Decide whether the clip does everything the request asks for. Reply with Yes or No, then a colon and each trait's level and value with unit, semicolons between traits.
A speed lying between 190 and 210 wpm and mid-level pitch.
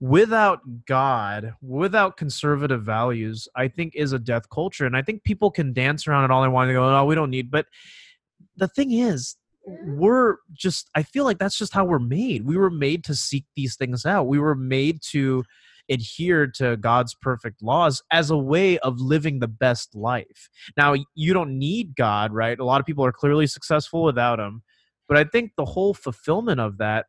Yes: average, 200 wpm; medium, 145 Hz